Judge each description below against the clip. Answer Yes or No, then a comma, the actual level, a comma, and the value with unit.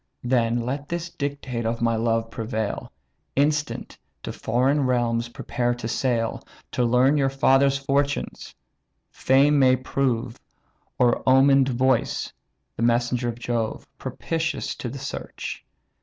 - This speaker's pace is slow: Yes, slow, 125 wpm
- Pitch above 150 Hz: No, low, 125 Hz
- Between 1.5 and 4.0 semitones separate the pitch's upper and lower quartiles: Yes, average, 2.8 semitones